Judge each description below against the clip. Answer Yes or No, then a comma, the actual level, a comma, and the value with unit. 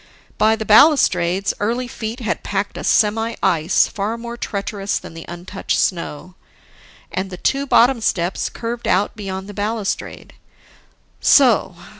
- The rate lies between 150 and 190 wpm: No, average, 140 wpm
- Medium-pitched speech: No, high, 205 Hz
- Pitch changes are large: No, average, 3.4 semitones